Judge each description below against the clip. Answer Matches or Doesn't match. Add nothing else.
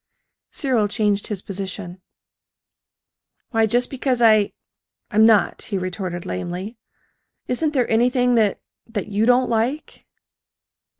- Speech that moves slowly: Matches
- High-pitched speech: Matches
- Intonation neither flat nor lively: Matches